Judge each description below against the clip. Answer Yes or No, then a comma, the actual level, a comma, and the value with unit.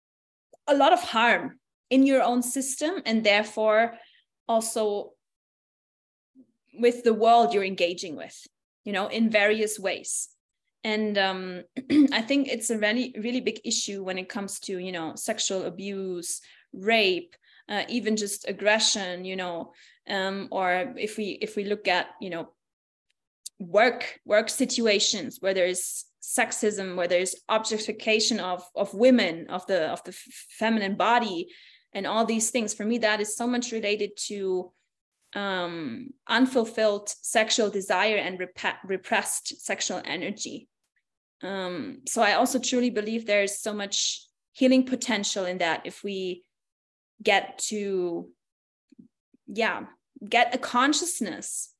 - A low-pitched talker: No, high, 215 Hz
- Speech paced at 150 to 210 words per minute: No, average, 140 wpm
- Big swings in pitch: No, average, 3.8 semitones